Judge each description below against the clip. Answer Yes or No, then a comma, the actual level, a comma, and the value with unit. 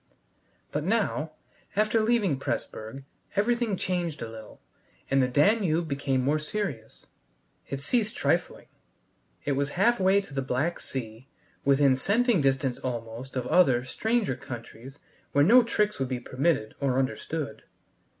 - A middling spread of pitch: No, wide, 7.3 semitones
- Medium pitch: Yes, medium, 145 Hz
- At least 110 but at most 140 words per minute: Yes, slow, 135 wpm